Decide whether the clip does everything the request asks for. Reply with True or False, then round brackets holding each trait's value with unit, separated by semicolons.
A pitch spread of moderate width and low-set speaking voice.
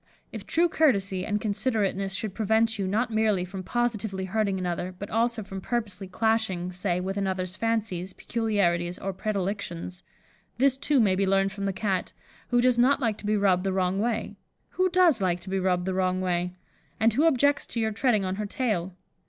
False (3.4 semitones; 200 Hz)